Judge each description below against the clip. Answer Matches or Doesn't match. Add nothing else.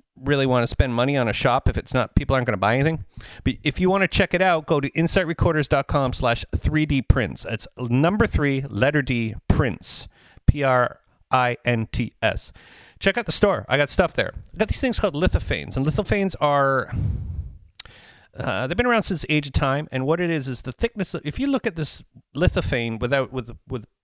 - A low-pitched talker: Matches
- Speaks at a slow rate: Doesn't match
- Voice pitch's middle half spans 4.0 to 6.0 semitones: Matches